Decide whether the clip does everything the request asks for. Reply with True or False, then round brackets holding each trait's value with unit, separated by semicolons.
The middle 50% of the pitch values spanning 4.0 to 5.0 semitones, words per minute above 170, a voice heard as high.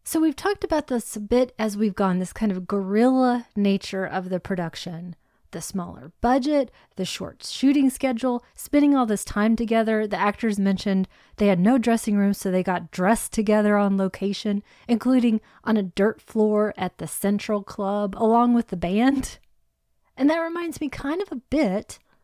True (4.3 semitones; 180 wpm; 215 Hz)